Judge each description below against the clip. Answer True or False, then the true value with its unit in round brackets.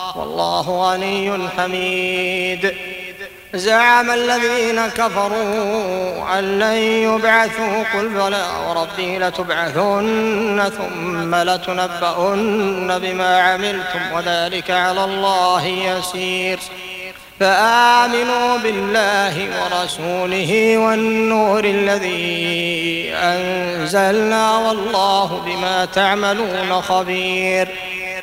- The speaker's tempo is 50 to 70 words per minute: True (65 wpm)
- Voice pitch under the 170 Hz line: False (185 Hz)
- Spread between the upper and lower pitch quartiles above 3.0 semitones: False (2.5 semitones)